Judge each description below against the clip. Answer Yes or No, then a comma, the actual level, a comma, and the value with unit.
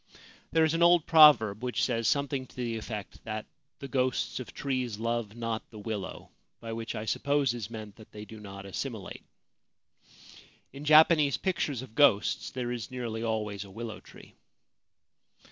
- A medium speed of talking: Yes, average, 175 wpm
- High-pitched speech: No, low, 115 Hz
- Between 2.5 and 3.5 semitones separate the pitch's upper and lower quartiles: No, average, 4.2 semitones